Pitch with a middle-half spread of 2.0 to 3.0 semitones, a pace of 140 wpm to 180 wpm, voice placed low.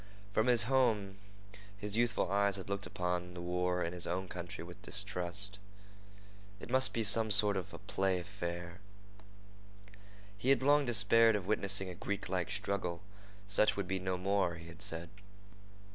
Yes: average, 2.7 semitones; average, 160 wpm; very low, 95 Hz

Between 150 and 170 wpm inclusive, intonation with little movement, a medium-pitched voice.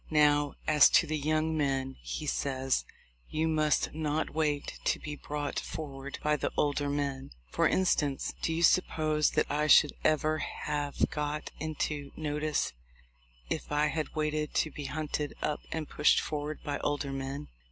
Yes: average, 160 wpm; narrow, 1.3 semitones; medium, 150 Hz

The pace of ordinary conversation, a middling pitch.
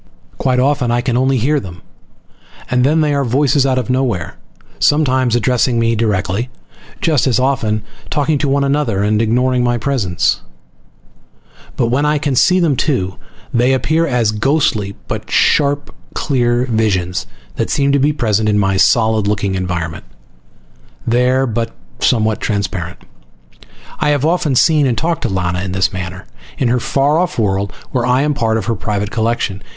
No: average, 165 wpm; low, 120 Hz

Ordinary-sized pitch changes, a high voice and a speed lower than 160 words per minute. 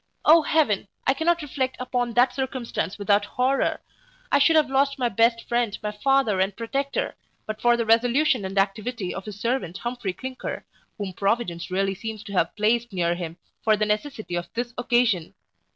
No: average, 4.5 semitones; high, 230 Hz; average, 180 wpm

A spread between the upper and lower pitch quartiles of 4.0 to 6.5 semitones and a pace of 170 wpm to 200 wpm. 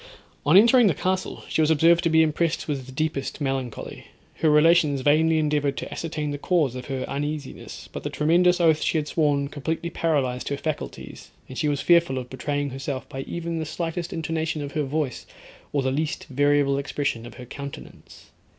No: average, 2.7 semitones; average, 185 wpm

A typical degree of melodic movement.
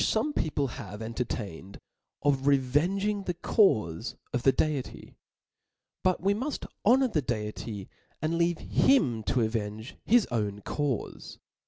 No: wide, 8.9 semitones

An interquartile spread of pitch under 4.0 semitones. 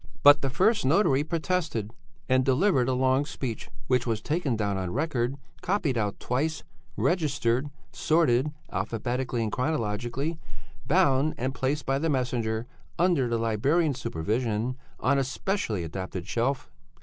No: average, 4.7 semitones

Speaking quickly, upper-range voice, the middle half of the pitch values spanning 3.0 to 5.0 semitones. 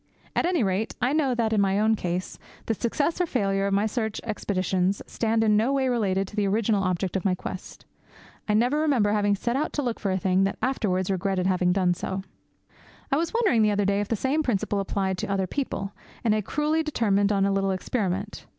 Yes: fast, 225 wpm; high, 205 Hz; average, 3.7 semitones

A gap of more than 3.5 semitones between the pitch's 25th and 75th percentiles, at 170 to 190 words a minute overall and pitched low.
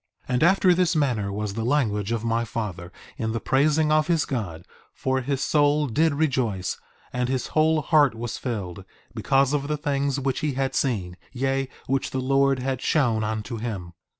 Yes: average, 4.5 semitones; average, 185 wpm; low, 130 Hz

